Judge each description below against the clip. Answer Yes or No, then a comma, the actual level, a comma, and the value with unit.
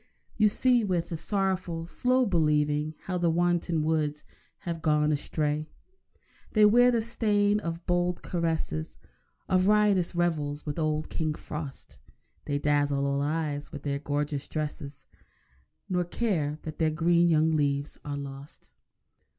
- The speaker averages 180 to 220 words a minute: No, average, 140 wpm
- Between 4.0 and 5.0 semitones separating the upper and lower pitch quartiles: No, average, 3.3 semitones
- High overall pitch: No, medium, 160 Hz